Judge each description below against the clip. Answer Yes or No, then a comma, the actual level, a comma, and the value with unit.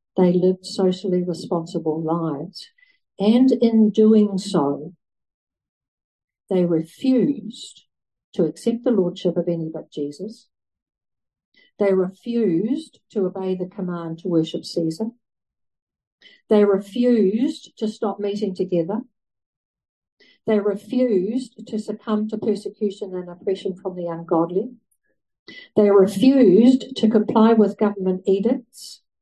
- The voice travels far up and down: No, average, 3.9 semitones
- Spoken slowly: Yes, slow, 105 wpm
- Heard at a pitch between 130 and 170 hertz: No, high, 205 Hz